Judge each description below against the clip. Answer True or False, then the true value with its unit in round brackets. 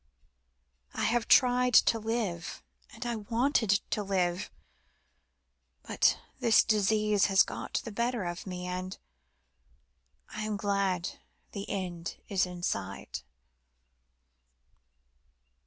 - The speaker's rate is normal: False (105 wpm)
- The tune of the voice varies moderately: True (3.6 semitones)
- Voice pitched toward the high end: True (205 Hz)